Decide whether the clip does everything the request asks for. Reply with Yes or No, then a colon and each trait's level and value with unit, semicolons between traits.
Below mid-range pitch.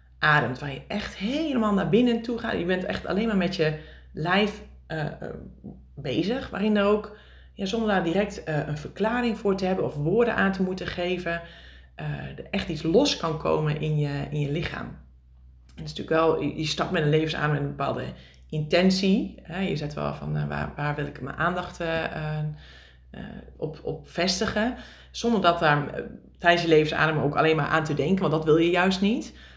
No: medium, 160 Hz